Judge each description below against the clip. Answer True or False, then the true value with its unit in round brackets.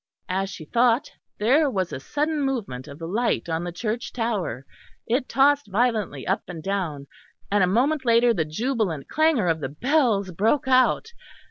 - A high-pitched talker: True (220 Hz)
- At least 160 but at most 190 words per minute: True (170 wpm)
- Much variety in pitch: True (6.8 semitones)